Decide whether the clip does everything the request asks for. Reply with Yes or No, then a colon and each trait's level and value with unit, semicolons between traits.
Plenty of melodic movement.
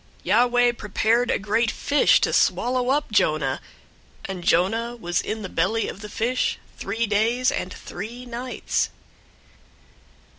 No: average, 3.5 semitones